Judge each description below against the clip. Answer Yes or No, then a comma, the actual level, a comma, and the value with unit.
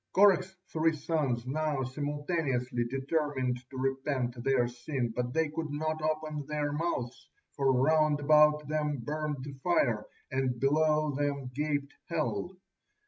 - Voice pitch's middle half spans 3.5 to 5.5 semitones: No, average, 2.9 semitones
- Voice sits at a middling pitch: Yes, medium, 145 Hz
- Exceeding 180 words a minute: No, slow, 135 wpm